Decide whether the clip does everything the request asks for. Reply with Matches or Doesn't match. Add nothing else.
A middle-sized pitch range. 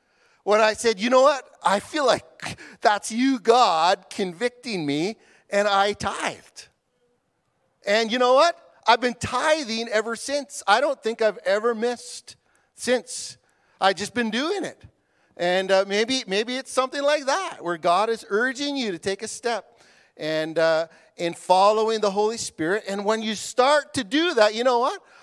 Matches